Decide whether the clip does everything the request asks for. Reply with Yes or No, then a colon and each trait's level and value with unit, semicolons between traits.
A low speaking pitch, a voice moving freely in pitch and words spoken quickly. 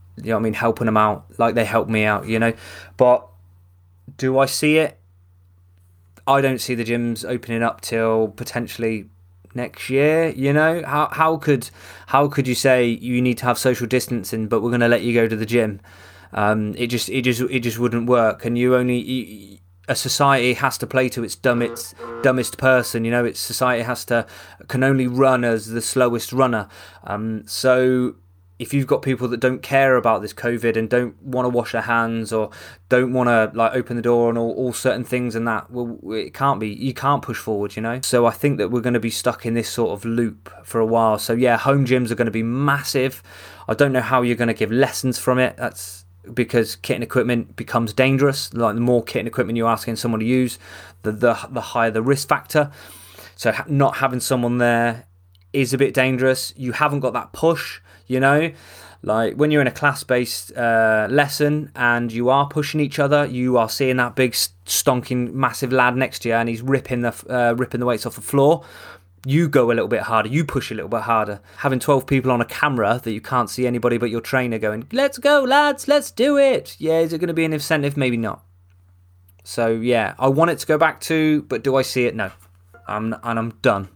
No: low, 120 Hz; average, 2.8 semitones; fast, 225 wpm